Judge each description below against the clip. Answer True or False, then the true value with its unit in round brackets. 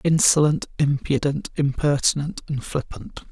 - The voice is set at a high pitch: False (145 Hz)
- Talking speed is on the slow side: True (90 wpm)